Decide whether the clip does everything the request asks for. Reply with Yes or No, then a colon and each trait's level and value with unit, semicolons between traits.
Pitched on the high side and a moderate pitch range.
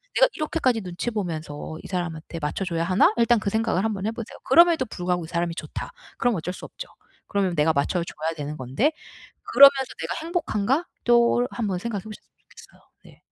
No: high, 200 Hz; wide, 6.1 semitones